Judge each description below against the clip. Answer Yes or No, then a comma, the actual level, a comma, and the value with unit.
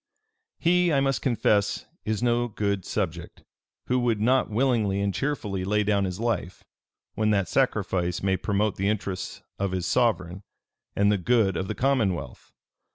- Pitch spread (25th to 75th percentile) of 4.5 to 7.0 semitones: No, average, 3.9 semitones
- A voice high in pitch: No, low, 105 Hz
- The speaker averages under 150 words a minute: No, average, 160 wpm